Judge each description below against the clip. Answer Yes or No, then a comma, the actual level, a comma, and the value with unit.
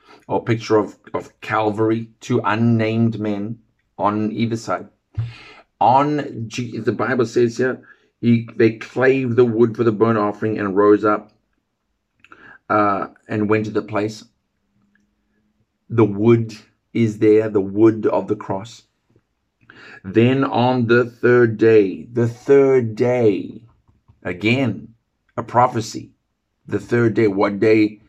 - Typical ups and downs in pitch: No, narrow, 1.8 semitones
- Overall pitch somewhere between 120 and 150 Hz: No, low, 110 Hz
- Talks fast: No, slow, 125 wpm